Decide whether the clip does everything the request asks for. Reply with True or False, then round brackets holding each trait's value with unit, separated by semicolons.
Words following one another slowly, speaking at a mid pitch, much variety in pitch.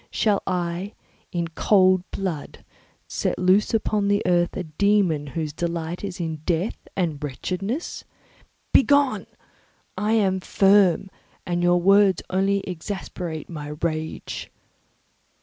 False (120 wpm; 180 Hz; 3.2 semitones)